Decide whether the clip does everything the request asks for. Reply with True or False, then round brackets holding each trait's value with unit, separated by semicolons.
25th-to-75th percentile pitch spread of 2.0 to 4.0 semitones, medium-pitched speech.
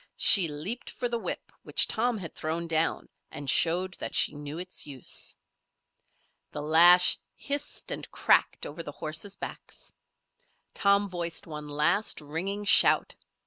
False (4.7 semitones; 170 Hz)